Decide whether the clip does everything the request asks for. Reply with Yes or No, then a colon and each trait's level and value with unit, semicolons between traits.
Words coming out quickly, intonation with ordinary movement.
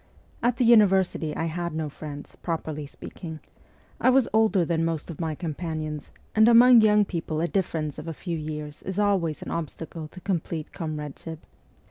No: average, 175 wpm; average, 3.8 semitones